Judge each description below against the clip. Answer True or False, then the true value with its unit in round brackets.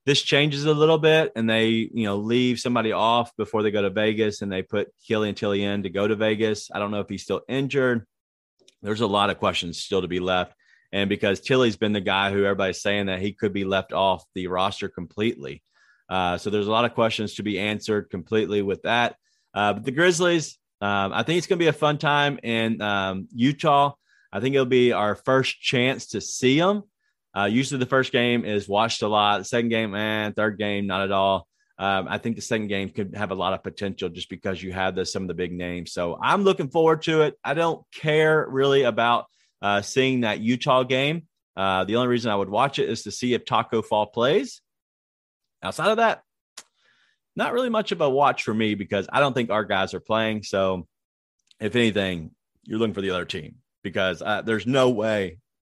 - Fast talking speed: True (225 wpm)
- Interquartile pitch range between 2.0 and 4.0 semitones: False (4.6 semitones)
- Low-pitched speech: True (110 Hz)